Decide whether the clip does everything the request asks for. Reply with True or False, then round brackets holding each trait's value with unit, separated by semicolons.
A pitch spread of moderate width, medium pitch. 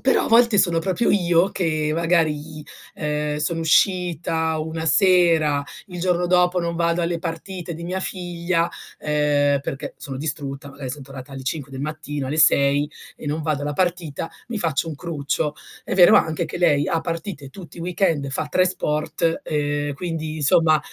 True (3.0 semitones; 160 Hz)